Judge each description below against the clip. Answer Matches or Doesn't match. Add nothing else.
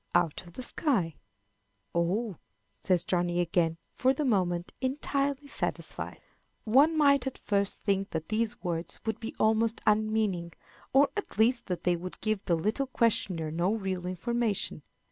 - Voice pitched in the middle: Doesn't match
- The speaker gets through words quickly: Doesn't match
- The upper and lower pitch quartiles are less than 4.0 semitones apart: Doesn't match